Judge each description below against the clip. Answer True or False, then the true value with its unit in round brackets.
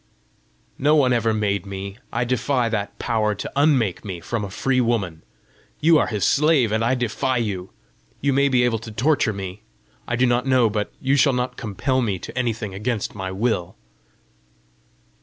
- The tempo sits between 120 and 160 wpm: False (180 wpm)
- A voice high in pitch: False (115 Hz)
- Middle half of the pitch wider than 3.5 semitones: True (3.9 semitones)